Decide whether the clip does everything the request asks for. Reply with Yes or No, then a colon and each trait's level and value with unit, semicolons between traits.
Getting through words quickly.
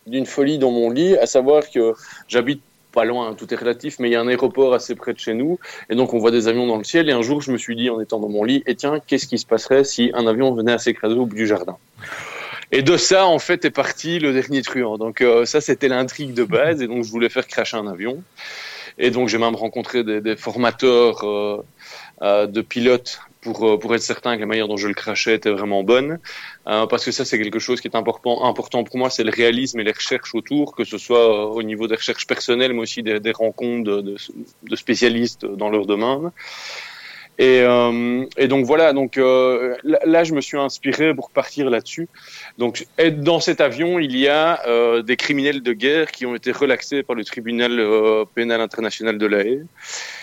Yes: fast, 235 wpm